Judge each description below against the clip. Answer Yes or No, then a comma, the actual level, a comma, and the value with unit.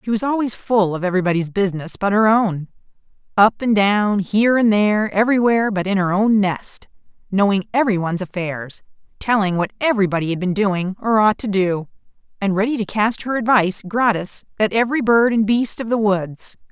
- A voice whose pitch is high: Yes, high, 205 Hz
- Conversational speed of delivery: Yes, average, 175 wpm